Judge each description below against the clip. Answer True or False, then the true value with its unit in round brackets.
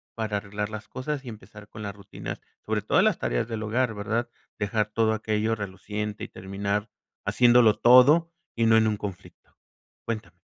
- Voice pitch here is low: True (110 Hz)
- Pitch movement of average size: False (2.0 semitones)